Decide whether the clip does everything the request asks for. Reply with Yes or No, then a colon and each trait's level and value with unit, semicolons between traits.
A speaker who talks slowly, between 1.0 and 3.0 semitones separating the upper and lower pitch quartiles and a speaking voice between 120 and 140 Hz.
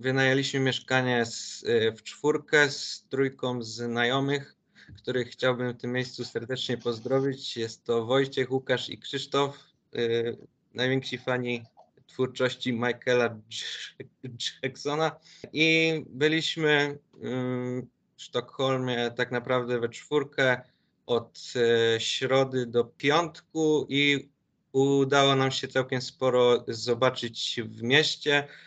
Yes: slow, 105 wpm; narrow, 2.4 semitones; low, 130 Hz